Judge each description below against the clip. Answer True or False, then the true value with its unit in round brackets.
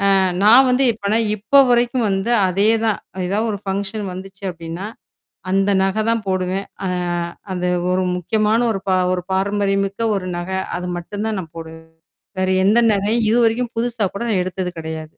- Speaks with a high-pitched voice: True (195 Hz)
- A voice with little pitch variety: False (3.1 semitones)